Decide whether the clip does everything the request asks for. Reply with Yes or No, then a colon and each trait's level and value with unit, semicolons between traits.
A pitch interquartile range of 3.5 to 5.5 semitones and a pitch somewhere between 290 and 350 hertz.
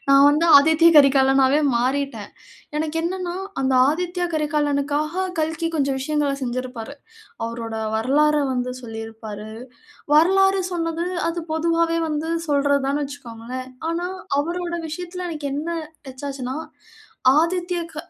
Yes: average, 4.1 semitones; very high, 295 Hz